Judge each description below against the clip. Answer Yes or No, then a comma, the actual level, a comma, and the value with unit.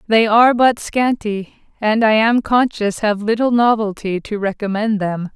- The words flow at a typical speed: Yes, average, 155 wpm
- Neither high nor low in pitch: No, high, 215 Hz